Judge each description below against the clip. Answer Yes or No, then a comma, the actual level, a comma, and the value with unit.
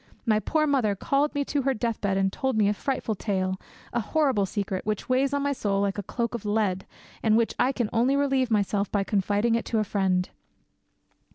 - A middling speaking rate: No, fast, 215 wpm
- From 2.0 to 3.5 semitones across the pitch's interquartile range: No, average, 4.7 semitones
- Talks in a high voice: Yes, high, 220 Hz